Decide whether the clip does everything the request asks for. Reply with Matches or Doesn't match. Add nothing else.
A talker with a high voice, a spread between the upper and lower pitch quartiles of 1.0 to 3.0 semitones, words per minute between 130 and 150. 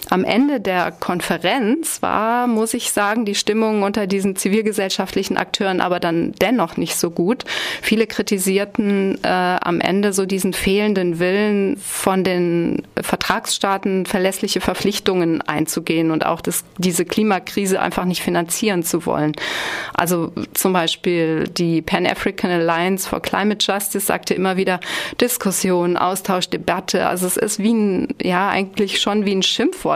Matches